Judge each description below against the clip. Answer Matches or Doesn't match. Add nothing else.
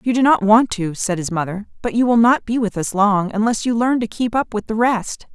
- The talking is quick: Matches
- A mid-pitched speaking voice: Doesn't match